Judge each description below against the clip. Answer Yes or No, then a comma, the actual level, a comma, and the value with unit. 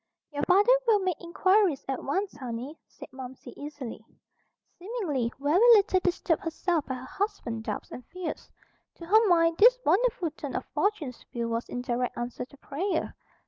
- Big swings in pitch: Yes, wide, 6.9 semitones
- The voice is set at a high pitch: Yes, very high, 325 Hz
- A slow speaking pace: No, average, 165 wpm